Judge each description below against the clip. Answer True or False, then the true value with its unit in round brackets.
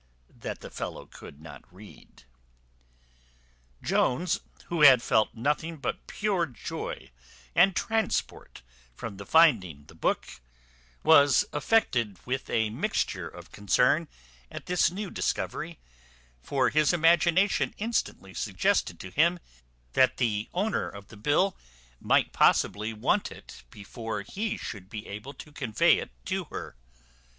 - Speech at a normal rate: False (130 wpm)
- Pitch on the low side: True (130 Hz)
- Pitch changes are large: True (8.3 semitones)